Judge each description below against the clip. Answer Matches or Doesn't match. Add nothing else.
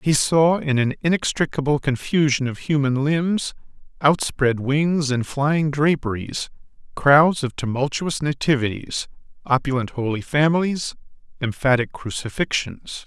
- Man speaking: Matches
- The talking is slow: Matches